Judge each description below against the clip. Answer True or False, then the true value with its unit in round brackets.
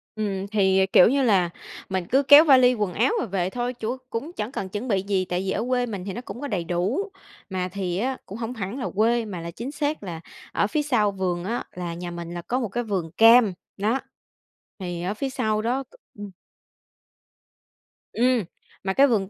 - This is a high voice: True (210 Hz)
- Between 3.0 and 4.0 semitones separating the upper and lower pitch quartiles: False (4.8 semitones)